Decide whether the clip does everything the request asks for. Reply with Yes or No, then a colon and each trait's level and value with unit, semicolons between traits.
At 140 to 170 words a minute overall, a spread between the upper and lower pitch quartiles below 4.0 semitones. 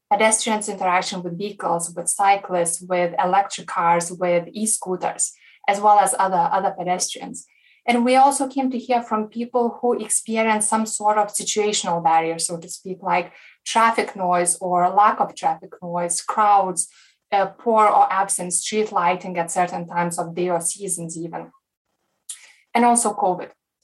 Yes: average, 155 wpm; average, 3.6 semitones